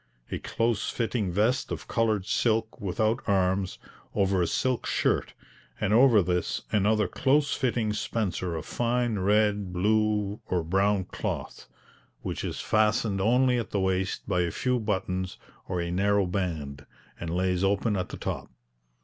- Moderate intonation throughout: Yes, average, 3.2 semitones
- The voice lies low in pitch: Yes, low, 100 Hz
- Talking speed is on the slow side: No, average, 150 wpm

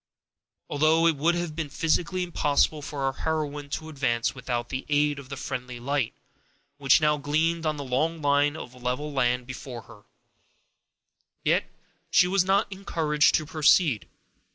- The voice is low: No, medium, 145 Hz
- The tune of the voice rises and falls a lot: No, average, 3.1 semitones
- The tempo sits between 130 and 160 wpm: Yes, average, 155 wpm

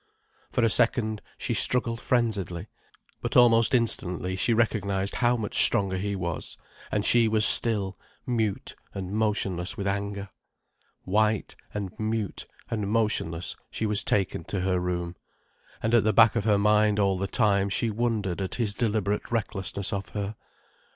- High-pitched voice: No, low, 105 Hz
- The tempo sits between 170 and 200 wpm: No, average, 155 wpm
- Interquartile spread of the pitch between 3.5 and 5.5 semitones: No, narrow, 2.5 semitones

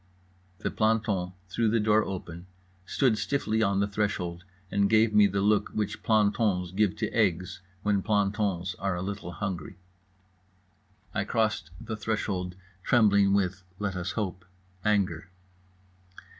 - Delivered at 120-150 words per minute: Yes, average, 140 wpm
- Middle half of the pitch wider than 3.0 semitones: No, narrow, 2.6 semitones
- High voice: No, low, 100 Hz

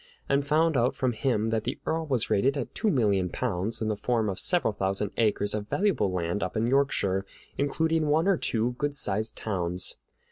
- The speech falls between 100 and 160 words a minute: No, average, 200 wpm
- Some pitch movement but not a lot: No, wide, 5.8 semitones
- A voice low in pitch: Yes, low, 115 Hz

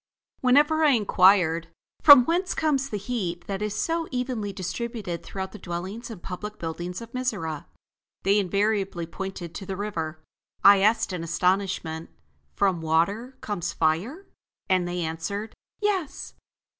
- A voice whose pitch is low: No, high, 200 Hz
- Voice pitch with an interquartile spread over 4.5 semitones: Yes, average, 5.2 semitones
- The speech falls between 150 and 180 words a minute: No, average, 140 wpm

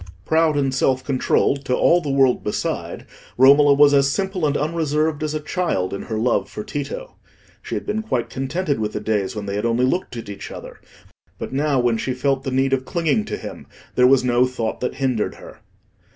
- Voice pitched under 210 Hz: Yes, low, 135 Hz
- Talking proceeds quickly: Yes, fast, 210 wpm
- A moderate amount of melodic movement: Yes, average, 3.4 semitones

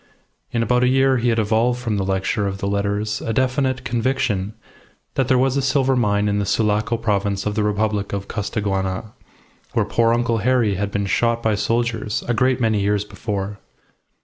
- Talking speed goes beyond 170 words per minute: Yes, average, 190 wpm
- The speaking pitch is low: Yes, low, 110 Hz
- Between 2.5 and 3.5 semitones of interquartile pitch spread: Yes, average, 3.1 semitones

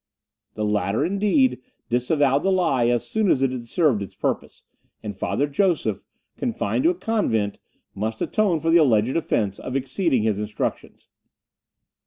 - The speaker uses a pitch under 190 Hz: Yes, low, 135 Hz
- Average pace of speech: Yes, average, 155 wpm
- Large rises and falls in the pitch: Yes, wide, 8.7 semitones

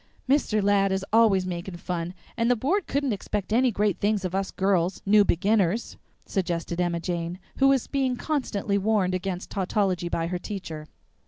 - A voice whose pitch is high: Yes, high, 195 Hz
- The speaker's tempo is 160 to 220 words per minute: Yes, average, 170 wpm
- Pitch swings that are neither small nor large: Yes, average, 3.6 semitones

